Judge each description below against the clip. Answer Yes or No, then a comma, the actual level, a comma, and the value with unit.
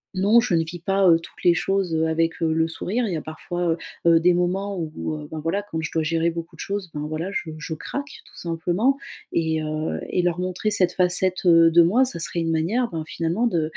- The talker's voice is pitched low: No, medium, 170 Hz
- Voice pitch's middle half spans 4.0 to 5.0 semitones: No, average, 2.7 semitones